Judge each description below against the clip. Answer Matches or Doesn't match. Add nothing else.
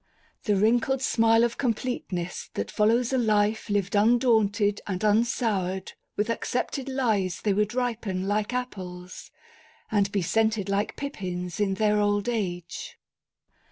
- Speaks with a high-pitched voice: Matches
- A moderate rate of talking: Doesn't match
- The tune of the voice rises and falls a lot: Doesn't match